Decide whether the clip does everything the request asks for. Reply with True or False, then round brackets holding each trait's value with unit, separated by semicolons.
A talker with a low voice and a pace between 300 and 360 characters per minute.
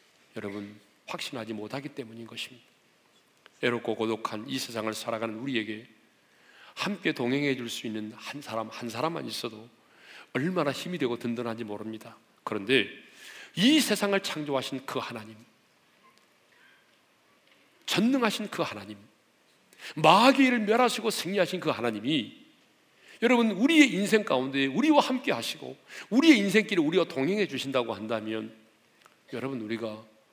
True (130 Hz; 305 characters per minute)